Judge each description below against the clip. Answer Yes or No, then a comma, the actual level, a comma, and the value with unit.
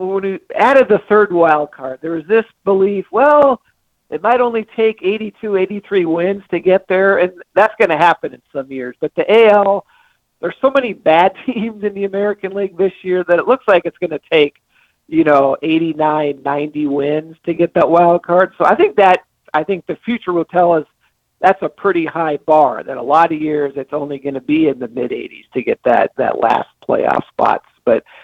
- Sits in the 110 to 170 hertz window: No, medium, 180 Hz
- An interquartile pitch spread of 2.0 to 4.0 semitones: No, average, 5.0 semitones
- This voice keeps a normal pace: No, fast, 215 wpm